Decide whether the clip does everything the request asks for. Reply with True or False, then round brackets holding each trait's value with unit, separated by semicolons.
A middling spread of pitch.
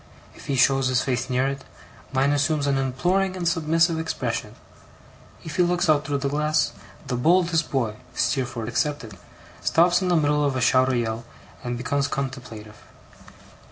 True (4.0 semitones)